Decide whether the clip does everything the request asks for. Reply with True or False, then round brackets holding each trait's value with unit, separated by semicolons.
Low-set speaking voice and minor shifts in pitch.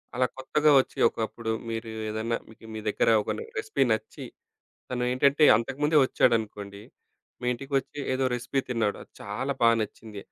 False (120 Hz; 3.5 semitones)